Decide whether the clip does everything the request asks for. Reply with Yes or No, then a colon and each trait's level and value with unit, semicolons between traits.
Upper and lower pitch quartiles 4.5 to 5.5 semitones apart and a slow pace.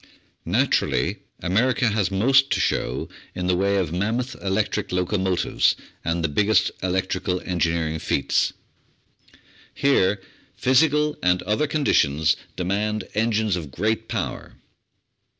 No: average, 3.8 semitones; slow, 115 wpm